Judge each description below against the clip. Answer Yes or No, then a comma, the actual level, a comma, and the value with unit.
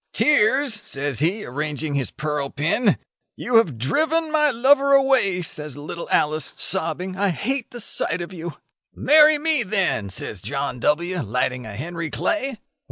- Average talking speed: Yes, average, 155 wpm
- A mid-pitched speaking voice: Yes, medium, 180 Hz